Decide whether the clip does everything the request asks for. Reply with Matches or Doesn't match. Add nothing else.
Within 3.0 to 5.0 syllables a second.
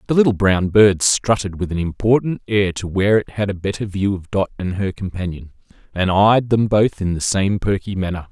Doesn't match